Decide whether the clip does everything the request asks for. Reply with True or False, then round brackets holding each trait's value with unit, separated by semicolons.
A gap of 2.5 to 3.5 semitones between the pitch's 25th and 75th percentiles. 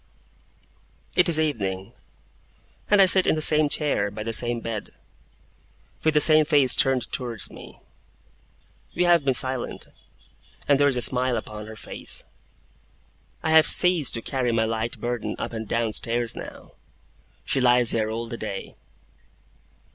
False (4.8 semitones)